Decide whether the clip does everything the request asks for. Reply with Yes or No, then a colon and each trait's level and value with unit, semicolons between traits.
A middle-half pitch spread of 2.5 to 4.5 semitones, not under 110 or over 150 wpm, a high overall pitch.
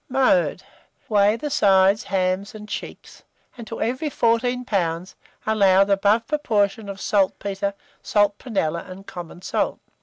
Yes: average, 3.1 semitones; average, 140 wpm; high, 205 Hz